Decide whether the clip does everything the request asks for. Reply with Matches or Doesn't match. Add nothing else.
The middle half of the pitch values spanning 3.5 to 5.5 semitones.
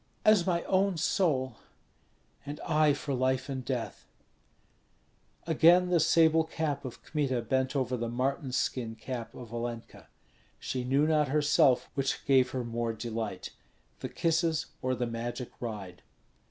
Matches